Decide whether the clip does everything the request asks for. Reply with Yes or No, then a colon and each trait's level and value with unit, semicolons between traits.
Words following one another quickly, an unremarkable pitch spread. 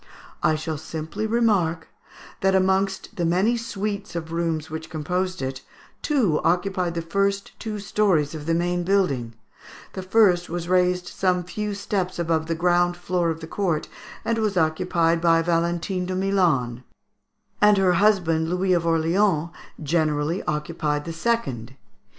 No: average, 150 wpm; average, 3.0 semitones